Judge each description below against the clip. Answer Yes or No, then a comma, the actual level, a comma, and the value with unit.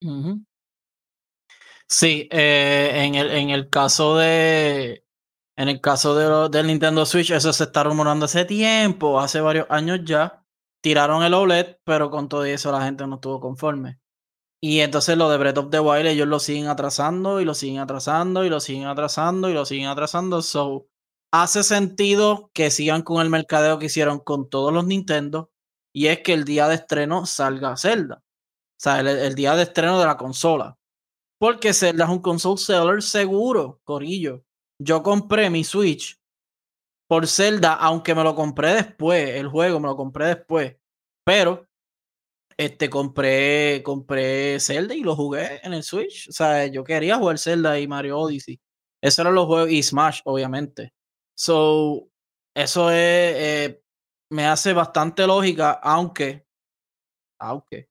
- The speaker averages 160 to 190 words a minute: Yes, average, 165 wpm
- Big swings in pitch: No, average, 3.3 semitones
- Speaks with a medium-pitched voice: Yes, medium, 155 Hz